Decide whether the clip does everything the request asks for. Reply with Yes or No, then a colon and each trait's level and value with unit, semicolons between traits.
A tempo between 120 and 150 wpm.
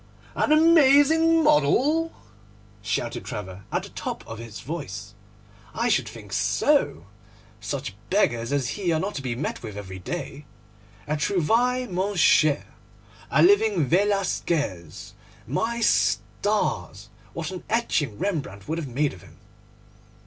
Yes: slow, 135 wpm